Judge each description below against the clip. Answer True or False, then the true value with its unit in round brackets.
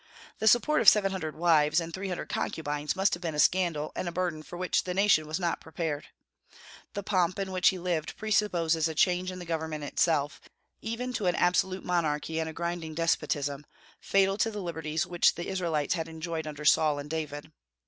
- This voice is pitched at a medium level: True (170 Hz)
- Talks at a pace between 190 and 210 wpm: True (200 wpm)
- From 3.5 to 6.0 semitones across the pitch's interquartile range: False (3.0 semitones)